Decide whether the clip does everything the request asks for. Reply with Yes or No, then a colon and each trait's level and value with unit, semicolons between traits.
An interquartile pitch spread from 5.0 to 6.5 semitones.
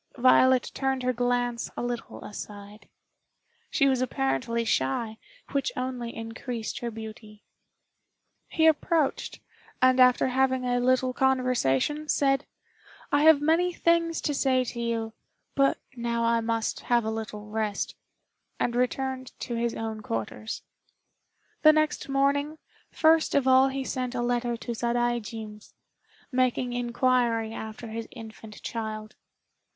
No: average, 2.8 semitones